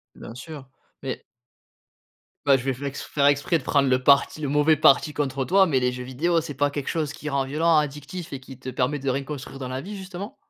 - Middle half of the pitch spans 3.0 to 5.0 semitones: No, narrow, 2.6 semitones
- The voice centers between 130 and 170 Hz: Yes, medium, 140 Hz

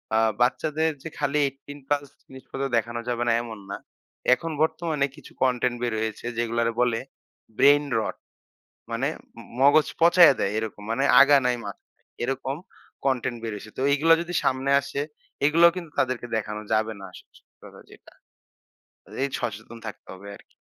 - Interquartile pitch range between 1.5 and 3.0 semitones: No, average, 4.0 semitones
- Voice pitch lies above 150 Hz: No, low, 130 Hz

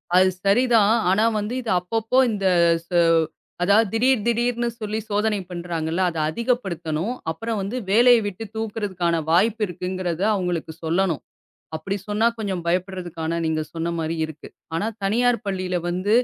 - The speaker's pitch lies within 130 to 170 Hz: No, high, 195 Hz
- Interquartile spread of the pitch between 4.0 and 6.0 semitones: Yes, average, 4.4 semitones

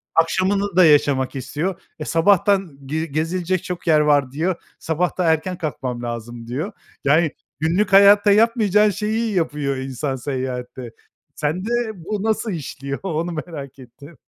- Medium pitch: Yes, medium, 160 Hz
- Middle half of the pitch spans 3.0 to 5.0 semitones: No, wide, 5.4 semitones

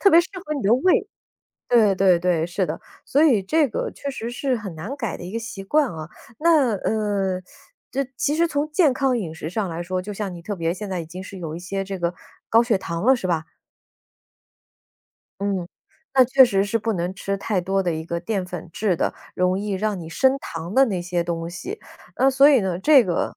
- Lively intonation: Yes, wide, 6.2 semitones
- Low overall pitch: No, high, 195 Hz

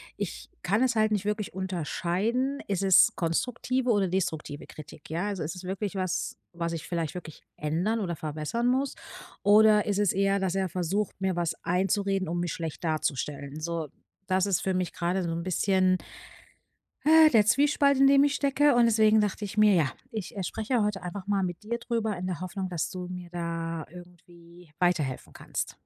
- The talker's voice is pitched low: No, high, 190 Hz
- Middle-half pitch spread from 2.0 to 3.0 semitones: No, average, 3.7 semitones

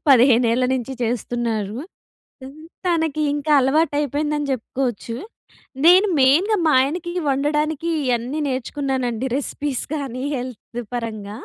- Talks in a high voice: Yes, very high, 265 Hz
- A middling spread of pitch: Yes, average, 3.7 semitones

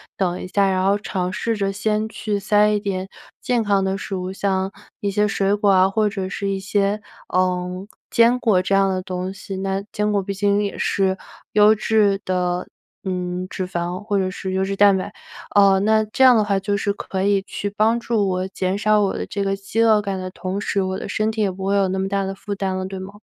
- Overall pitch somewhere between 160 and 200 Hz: Yes, high, 195 Hz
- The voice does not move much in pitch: Yes, narrow, 1.7 semitones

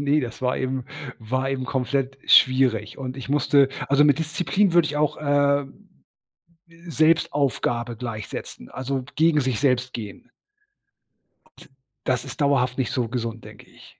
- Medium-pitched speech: No, low, 130 Hz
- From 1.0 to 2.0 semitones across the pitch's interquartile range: No, narrow, 2.4 semitones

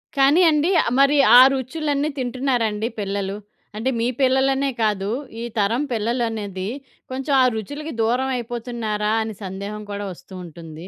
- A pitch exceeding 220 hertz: Yes, high, 235 Hz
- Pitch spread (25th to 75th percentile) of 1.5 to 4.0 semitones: No, average, 4.5 semitones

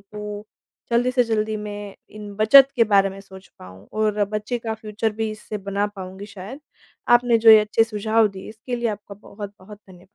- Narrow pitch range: Yes, narrow, 1.8 semitones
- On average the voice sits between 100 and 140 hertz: No, high, 210 Hz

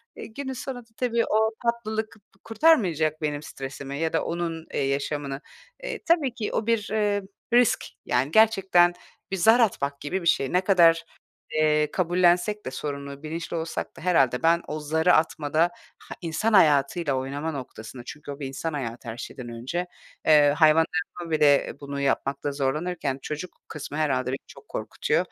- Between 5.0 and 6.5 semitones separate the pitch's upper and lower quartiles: Yes, average, 5.3 semitones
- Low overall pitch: No, medium, 160 Hz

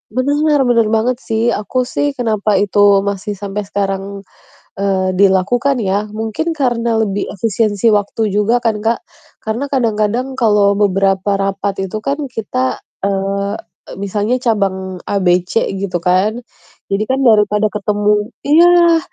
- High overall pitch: Yes, high, 210 Hz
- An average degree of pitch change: Yes, average, 3.1 semitones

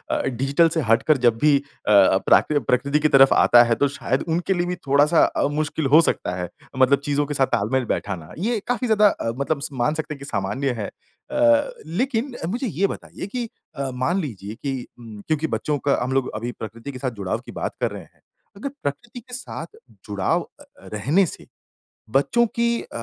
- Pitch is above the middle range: No, medium, 140 Hz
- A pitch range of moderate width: No, wide, 6.5 semitones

